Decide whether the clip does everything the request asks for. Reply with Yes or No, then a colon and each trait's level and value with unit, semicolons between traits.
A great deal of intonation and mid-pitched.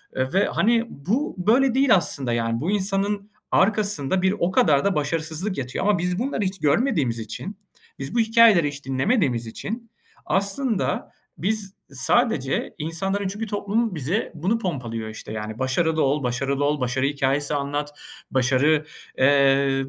Yes: wide, 7.1 semitones; medium, 160 Hz